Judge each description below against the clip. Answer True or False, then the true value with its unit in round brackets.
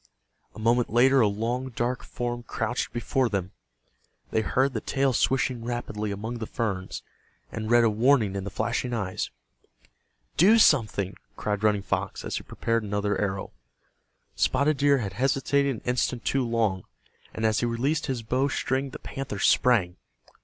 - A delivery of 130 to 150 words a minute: False (160 wpm)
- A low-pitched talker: True (120 Hz)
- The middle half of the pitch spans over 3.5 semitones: True (3.9 semitones)